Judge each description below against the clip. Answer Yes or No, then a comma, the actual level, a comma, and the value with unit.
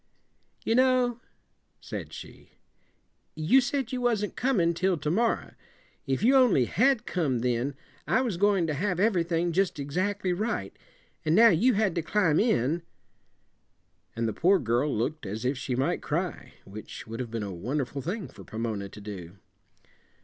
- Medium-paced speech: Yes, average, 165 wpm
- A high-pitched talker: No, medium, 170 Hz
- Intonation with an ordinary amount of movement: No, wide, 8.8 semitones